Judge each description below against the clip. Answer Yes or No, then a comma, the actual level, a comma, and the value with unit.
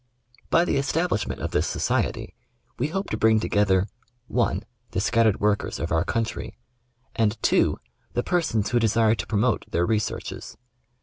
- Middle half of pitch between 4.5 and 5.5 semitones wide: No, average, 3.0 semitones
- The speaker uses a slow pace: No, average, 160 wpm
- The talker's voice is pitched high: No, low, 110 Hz